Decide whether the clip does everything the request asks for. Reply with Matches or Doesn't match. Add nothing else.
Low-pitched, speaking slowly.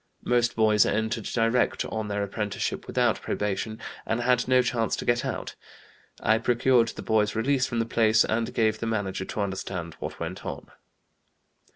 Doesn't match